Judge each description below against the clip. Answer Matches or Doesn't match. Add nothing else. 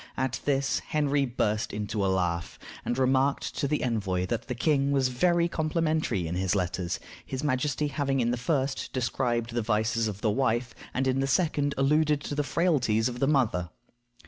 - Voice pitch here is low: Matches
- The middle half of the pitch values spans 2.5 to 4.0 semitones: Doesn't match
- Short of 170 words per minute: Doesn't match